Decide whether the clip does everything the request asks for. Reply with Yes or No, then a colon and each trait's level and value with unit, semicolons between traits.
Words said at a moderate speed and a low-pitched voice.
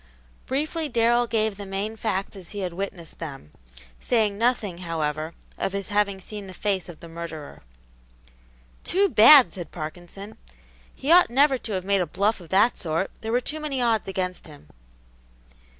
No: average, 170 wpm; high, 200 Hz